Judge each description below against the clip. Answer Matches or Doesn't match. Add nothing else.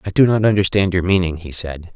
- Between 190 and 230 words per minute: Doesn't match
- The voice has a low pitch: Matches